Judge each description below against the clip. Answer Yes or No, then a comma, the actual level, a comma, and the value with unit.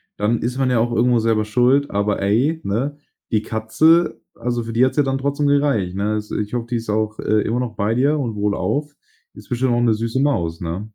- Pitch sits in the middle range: No, low, 115 Hz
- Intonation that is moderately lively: Yes, average, 3.7 semitones